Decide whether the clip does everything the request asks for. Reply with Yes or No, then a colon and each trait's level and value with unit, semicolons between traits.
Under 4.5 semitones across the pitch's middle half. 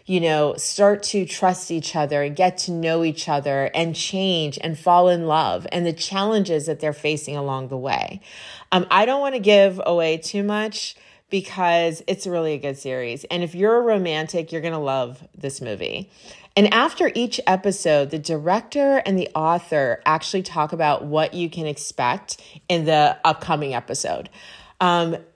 Yes: average, 3.8 semitones